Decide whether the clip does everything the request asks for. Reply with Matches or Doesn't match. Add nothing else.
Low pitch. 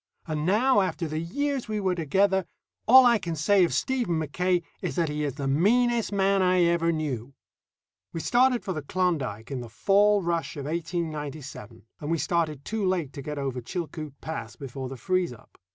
Doesn't match